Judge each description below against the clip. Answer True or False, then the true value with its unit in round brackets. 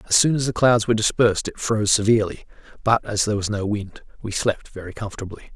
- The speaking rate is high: True (215 wpm)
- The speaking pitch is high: False (110 Hz)